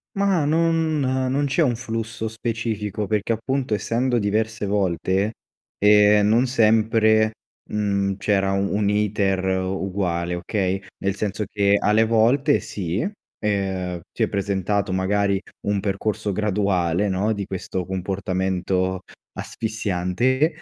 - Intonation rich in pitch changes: No, narrow, 2.6 semitones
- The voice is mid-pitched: No, low, 105 Hz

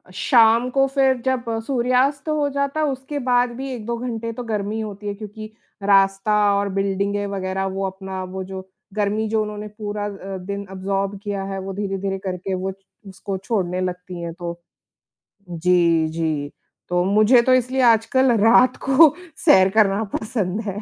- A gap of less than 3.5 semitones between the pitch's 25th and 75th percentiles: No, average, 3.8 semitones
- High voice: Yes, high, 205 Hz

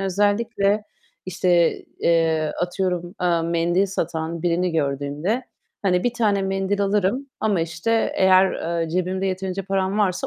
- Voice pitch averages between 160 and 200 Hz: Yes, medium, 185 Hz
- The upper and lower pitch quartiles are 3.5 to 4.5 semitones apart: No, average, 2.8 semitones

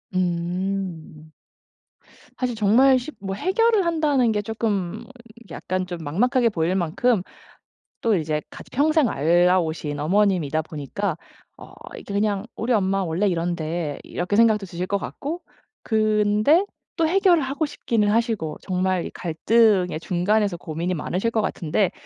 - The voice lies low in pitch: No, high, 195 Hz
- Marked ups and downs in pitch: No, average, 4.9 semitones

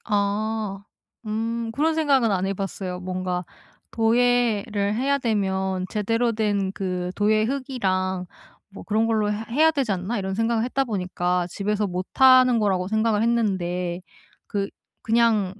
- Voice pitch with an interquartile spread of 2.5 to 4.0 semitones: Yes, average, 3.3 semitones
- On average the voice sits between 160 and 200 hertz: No, high, 210 Hz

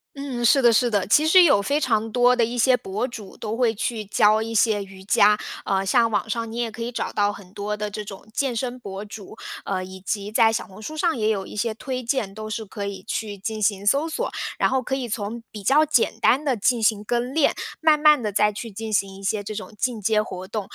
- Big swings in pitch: No, average, 3.2 semitones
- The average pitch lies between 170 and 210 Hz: No, high, 220 Hz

